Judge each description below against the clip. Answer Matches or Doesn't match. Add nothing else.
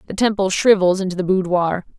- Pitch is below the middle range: Doesn't match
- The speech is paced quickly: Doesn't match